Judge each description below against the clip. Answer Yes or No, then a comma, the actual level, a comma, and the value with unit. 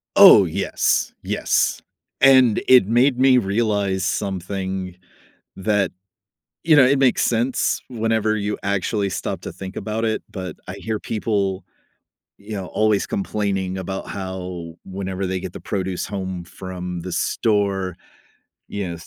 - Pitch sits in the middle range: No, low, 100 Hz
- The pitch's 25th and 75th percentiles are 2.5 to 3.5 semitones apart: Yes, average, 2.9 semitones